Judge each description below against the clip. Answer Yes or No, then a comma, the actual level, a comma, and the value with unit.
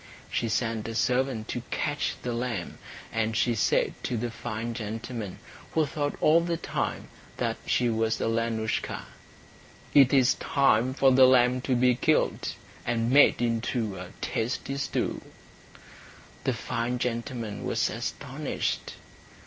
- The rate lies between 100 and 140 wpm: Yes, slow, 135 wpm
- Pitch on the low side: Yes, low, 120 Hz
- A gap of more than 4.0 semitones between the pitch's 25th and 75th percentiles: No, narrow, 2.4 semitones